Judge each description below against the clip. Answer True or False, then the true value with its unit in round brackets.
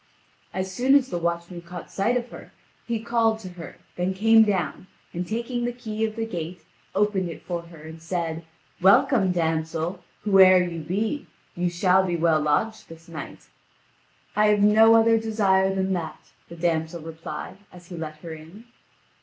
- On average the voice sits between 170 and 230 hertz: True (185 Hz)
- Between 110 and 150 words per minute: False (175 wpm)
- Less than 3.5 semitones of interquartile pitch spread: False (4.4 semitones)